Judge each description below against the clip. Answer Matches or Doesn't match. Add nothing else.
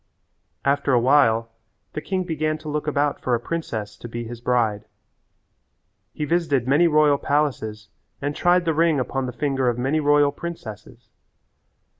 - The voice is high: Doesn't match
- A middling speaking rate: Matches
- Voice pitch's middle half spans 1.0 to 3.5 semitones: Doesn't match